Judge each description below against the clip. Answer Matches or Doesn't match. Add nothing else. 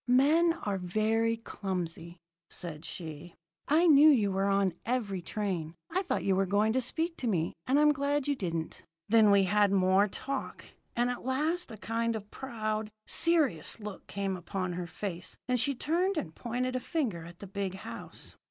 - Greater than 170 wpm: Matches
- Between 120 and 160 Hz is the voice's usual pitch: Doesn't match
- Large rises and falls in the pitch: Matches